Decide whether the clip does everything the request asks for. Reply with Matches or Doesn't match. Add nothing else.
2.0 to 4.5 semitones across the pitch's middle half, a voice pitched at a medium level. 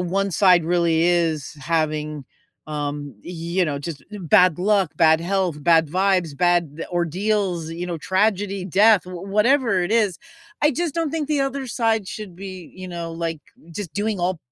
Matches